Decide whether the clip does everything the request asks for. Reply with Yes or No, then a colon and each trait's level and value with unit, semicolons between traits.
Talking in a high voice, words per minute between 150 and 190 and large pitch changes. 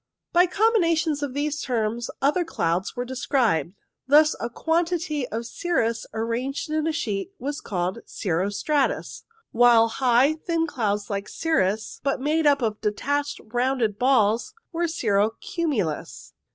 No: very high, 260 Hz; average, 140 wpm; wide, 6.0 semitones